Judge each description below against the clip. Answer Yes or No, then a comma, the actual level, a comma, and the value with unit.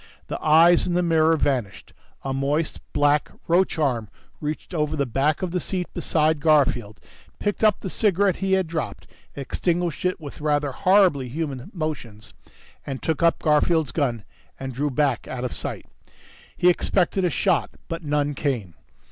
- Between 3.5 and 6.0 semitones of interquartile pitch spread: Yes, average, 4.0 semitones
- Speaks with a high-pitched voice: No, medium, 150 Hz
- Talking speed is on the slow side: No, average, 165 wpm